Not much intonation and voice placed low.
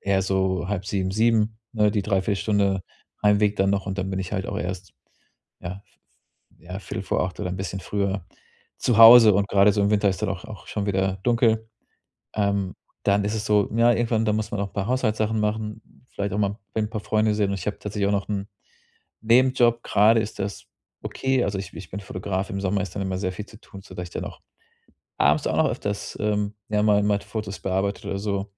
Yes: narrow, 1.8 semitones; low, 100 Hz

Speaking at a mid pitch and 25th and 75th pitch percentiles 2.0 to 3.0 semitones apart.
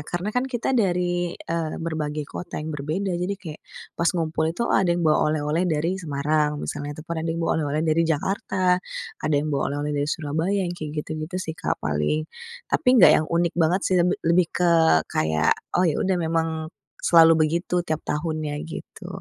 Yes: medium, 165 Hz; average, 2.7 semitones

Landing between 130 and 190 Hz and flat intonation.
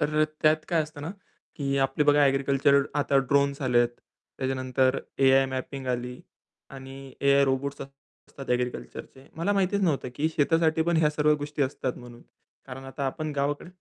Yes: medium, 140 Hz; narrow, 2.2 semitones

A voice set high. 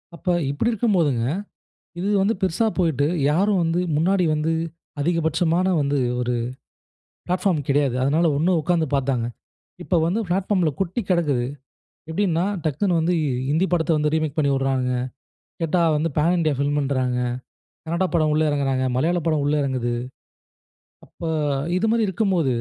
No: medium, 160 Hz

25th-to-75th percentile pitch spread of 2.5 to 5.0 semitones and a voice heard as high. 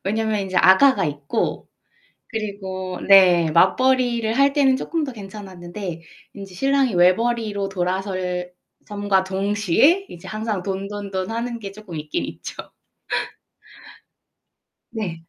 Yes: average, 3.4 semitones; high, 200 Hz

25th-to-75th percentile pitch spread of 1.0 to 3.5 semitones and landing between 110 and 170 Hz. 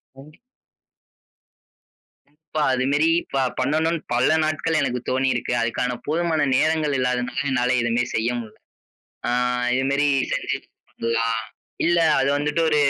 No: average, 3.9 semitones; low, 135 Hz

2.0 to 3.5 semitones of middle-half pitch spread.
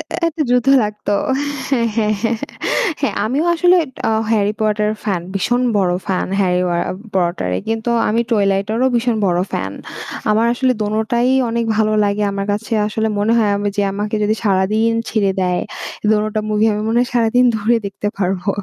Yes: narrow, 2.5 semitones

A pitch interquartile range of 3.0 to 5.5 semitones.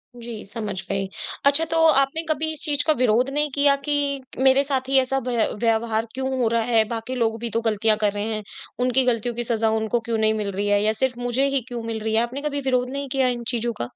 Yes: average, 3.3 semitones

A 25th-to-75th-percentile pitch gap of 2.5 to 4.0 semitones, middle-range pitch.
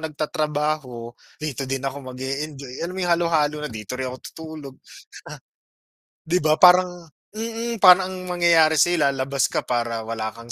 No: average, 4.6 semitones; medium, 150 Hz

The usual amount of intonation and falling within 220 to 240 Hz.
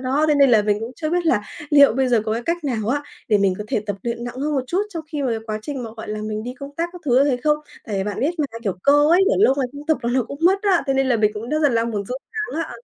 No: average, 5.0 semitones; very high, 260 Hz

